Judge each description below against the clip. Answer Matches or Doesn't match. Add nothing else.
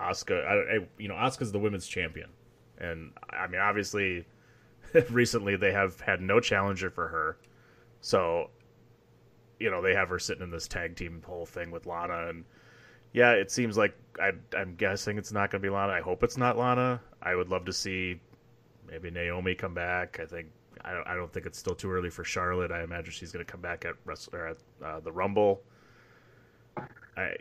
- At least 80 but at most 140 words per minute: Doesn't match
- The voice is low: Matches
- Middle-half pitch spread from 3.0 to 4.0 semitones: Doesn't match